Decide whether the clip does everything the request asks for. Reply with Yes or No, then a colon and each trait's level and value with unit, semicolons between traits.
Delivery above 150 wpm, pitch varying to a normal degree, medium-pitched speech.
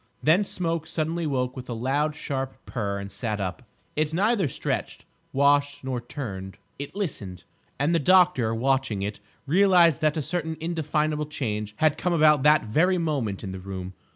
No: average, 170 wpm; wide, 6.1 semitones; medium, 145 Hz